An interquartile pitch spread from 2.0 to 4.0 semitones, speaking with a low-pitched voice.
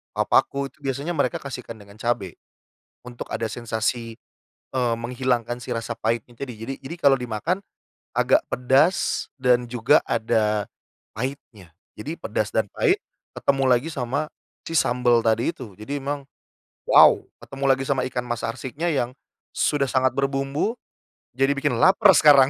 Yes: average, 3.0 semitones; low, 125 Hz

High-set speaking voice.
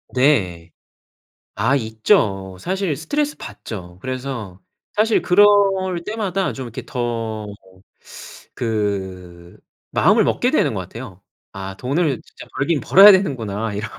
No: low, 120 Hz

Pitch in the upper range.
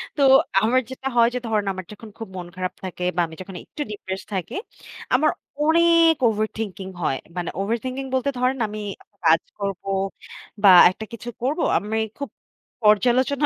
Yes: high, 220 Hz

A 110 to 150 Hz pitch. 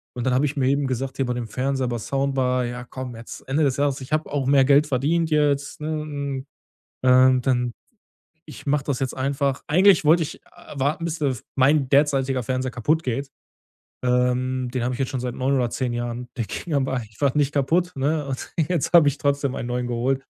Yes: low, 135 Hz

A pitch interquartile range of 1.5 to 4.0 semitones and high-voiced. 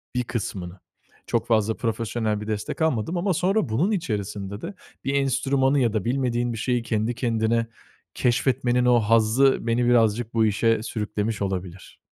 No: average, 2.9 semitones; low, 115 Hz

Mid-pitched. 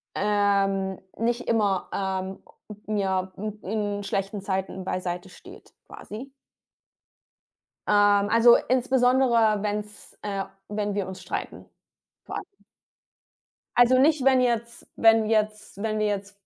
No: high, 210 Hz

